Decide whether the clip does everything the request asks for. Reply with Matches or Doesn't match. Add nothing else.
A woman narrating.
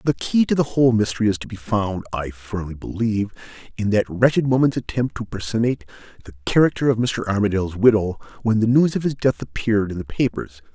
Doesn't match